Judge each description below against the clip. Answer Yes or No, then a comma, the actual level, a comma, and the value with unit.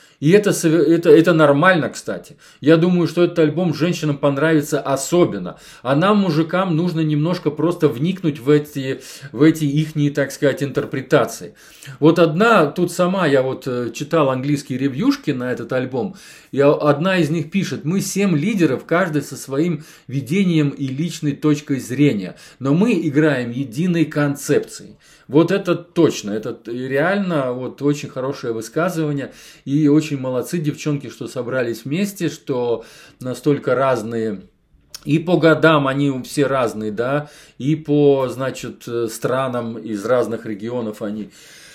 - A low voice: No, medium, 150 Hz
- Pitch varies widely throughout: No, average, 3.5 semitones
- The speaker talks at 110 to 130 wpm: No, average, 140 wpm